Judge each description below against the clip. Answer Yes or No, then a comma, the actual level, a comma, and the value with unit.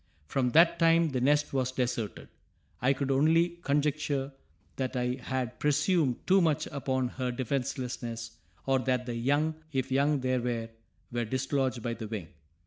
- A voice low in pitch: Yes, low, 130 Hz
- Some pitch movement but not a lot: Yes, average, 3.0 semitones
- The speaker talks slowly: No, average, 155 wpm